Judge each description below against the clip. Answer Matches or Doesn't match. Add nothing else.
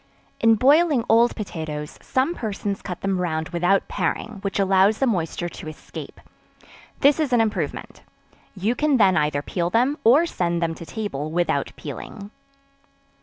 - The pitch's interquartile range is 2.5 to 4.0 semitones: Doesn't match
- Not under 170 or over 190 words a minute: Doesn't match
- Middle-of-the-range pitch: Doesn't match